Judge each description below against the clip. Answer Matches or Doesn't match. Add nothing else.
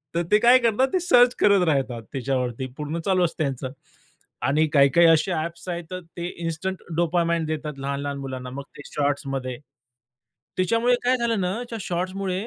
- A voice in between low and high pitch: Matches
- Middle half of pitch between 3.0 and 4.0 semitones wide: Doesn't match